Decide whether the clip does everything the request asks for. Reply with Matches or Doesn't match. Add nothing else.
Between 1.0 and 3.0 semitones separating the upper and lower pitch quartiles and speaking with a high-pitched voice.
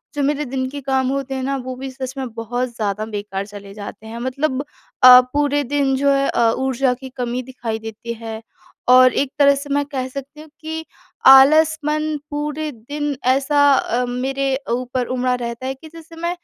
Matches